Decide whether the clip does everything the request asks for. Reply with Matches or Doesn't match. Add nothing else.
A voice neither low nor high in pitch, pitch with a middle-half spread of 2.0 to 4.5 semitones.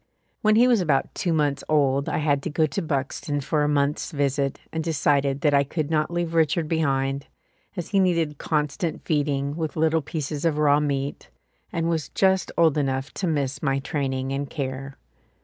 Matches